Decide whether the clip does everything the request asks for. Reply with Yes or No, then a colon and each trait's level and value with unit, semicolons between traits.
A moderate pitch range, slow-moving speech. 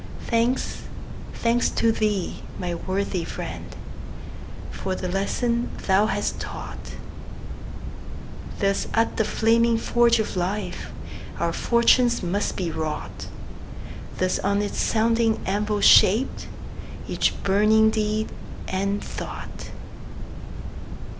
Yes: average, 3.0 semitones; slow, 100 wpm